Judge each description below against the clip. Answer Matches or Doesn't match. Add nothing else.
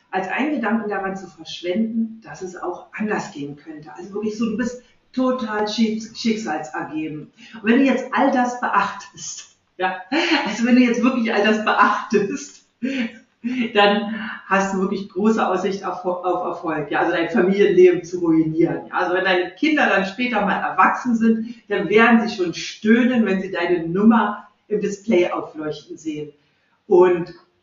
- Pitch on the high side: Matches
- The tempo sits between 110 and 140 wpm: Doesn't match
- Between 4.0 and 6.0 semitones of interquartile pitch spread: Matches